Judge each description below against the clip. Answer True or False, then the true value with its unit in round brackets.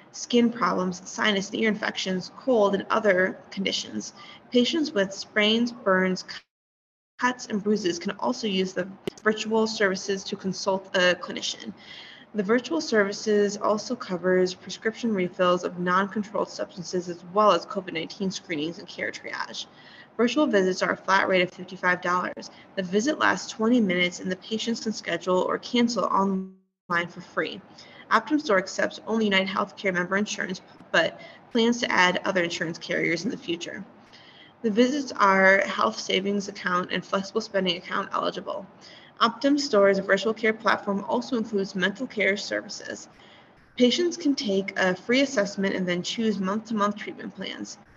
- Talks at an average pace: True (150 wpm)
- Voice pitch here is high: True (195 Hz)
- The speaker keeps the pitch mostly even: False (3.1 semitones)